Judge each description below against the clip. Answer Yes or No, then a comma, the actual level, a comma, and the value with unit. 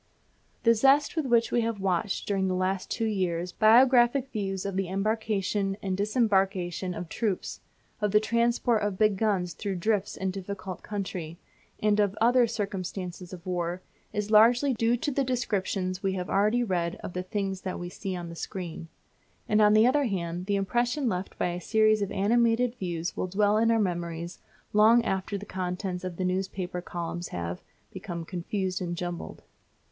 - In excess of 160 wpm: Yes, average, 180 wpm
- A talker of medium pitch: No, high, 195 Hz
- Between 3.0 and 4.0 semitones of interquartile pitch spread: Yes, average, 3.3 semitones